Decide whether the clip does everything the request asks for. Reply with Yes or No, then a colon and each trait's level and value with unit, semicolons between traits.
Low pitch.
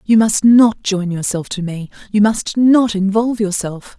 No: high, 205 Hz